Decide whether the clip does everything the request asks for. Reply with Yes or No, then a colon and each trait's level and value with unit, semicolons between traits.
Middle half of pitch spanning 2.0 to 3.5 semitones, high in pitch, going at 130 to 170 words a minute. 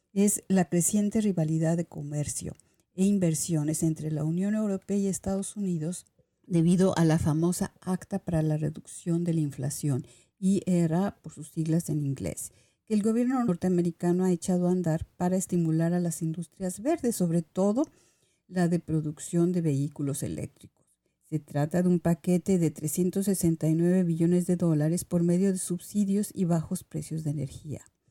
No: average, 2.8 semitones; medium, 175 Hz; average, 160 wpm